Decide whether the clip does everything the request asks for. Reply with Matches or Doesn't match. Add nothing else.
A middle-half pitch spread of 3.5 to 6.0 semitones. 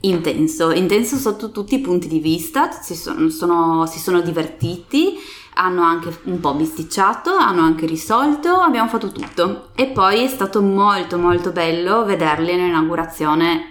Matches